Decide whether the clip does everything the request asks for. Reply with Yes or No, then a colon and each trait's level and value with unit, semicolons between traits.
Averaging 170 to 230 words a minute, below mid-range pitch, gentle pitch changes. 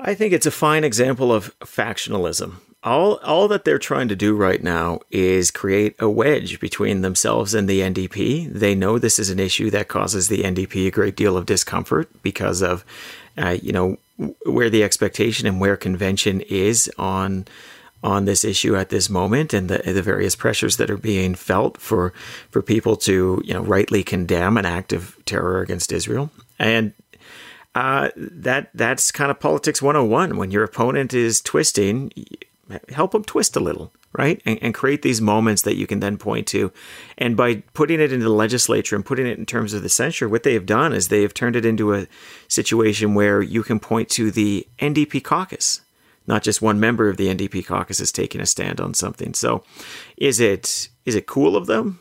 No: average, 195 wpm; low, 105 Hz; average, 3.4 semitones